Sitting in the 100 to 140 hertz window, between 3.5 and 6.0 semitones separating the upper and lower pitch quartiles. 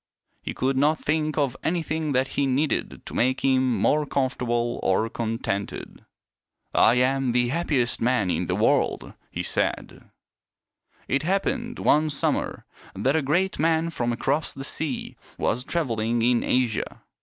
Yes: low, 135 Hz; average, 4.2 semitones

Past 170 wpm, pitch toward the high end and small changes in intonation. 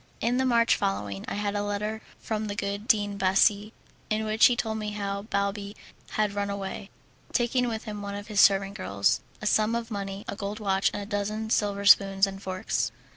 Yes: fast, 205 wpm; high, 205 Hz; narrow, 1.5 semitones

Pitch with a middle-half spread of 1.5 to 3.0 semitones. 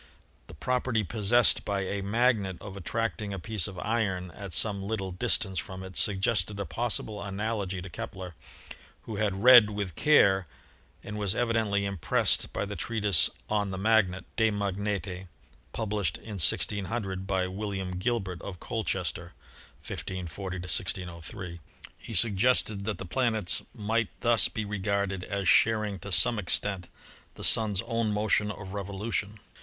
Yes: narrow, 2.6 semitones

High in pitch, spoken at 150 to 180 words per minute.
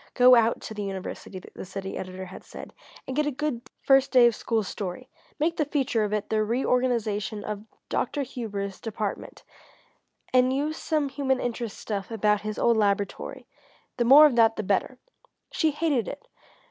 Yes: high, 230 Hz; average, 175 wpm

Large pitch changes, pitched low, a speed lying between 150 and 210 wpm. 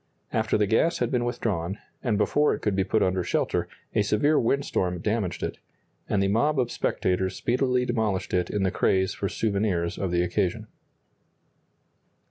No: average, 4.3 semitones; low, 105 Hz; average, 170 wpm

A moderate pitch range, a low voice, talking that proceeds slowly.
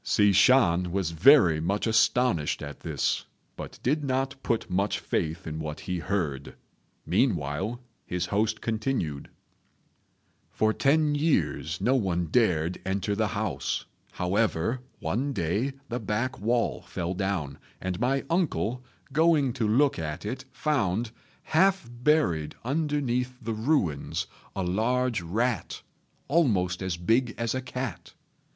No: wide, 6.4 semitones; low, 110 Hz; slow, 130 wpm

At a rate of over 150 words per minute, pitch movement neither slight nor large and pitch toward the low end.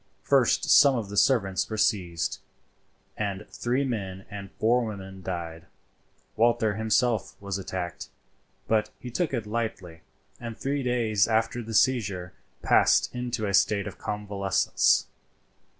No: slow, 135 wpm; average, 3.4 semitones; low, 105 Hz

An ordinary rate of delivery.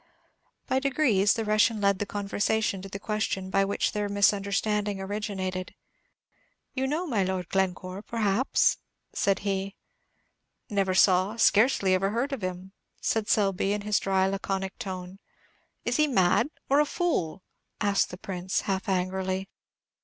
Yes: average, 145 wpm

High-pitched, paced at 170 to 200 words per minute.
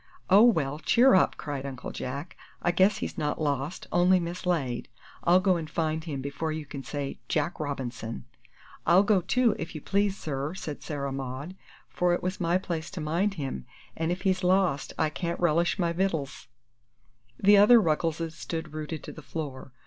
No: medium, 160 Hz; average, 180 wpm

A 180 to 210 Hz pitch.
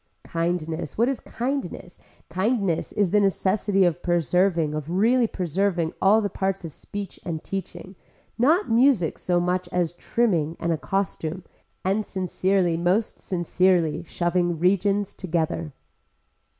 Yes: medium, 185 Hz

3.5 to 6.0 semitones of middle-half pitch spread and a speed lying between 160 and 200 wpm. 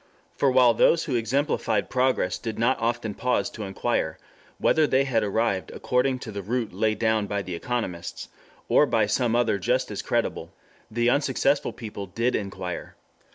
Yes: average, 3.8 semitones; average, 165 wpm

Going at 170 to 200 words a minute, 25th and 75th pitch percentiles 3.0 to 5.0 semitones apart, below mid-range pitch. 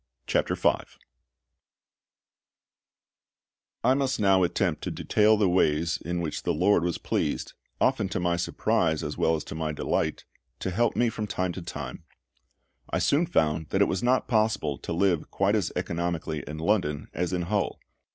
Yes: average, 180 wpm; average, 4.4 semitones; very low, 90 Hz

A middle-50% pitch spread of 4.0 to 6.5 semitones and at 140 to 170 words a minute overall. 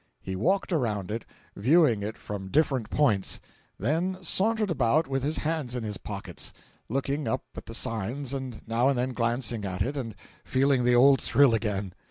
No: average, 4.5 semitones; average, 180 wpm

